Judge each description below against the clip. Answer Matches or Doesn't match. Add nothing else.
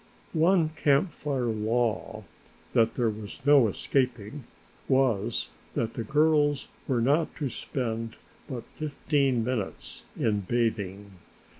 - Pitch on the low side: Matches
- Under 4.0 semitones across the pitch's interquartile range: Doesn't match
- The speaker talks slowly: Matches